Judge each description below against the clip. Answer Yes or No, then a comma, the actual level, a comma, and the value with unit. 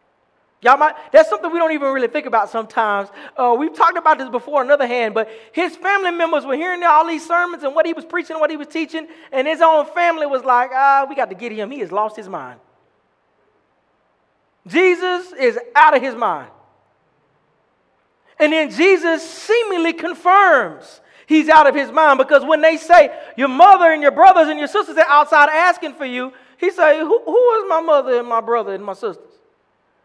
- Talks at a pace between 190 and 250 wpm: Yes, average, 200 wpm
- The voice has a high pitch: Yes, very high, 310 Hz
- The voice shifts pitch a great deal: No, average, 4.1 semitones